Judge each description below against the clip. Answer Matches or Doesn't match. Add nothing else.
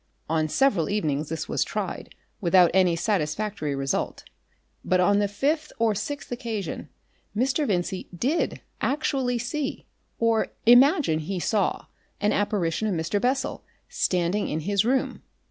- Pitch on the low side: Doesn't match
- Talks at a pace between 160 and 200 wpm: Doesn't match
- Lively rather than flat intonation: Matches